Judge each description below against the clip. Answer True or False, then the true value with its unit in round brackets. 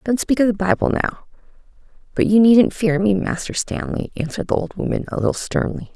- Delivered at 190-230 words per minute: True (200 wpm)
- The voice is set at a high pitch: True (210 Hz)